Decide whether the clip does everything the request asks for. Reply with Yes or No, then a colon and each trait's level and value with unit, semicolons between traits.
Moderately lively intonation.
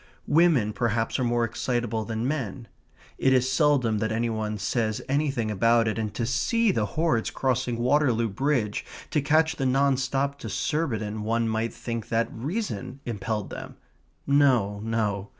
Yes: average, 3.8 semitones